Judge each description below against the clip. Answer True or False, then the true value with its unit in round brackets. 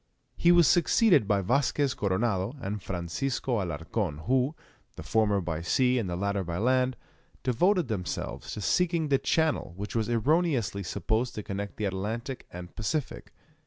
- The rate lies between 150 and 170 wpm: True (155 wpm)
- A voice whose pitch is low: True (110 Hz)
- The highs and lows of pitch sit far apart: True (5.7 semitones)